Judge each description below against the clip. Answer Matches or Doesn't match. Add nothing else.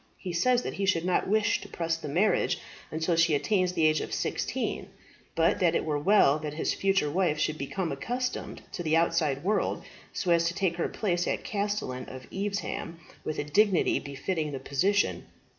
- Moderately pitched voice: Matches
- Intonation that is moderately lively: Matches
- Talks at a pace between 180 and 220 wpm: Matches